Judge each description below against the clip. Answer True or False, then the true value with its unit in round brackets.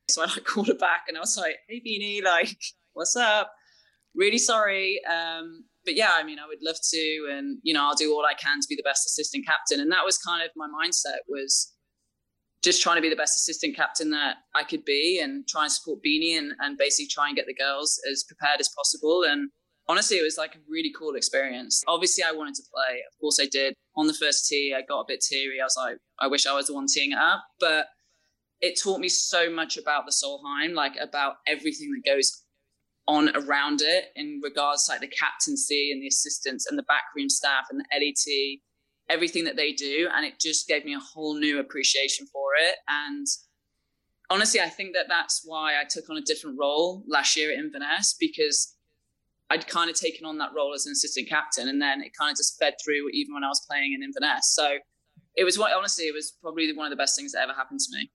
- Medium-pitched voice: True (155 Hz)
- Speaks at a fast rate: True (235 wpm)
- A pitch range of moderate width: False (6.5 semitones)